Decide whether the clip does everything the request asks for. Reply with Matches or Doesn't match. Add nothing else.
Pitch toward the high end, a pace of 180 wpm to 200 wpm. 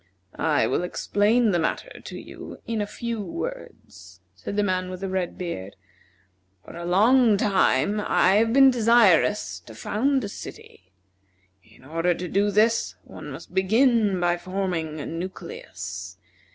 Doesn't match